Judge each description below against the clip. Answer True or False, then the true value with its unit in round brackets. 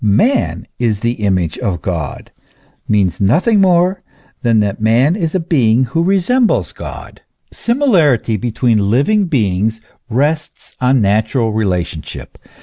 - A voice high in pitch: False (120 Hz)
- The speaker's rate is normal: False (130 wpm)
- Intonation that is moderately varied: False (8.2 semitones)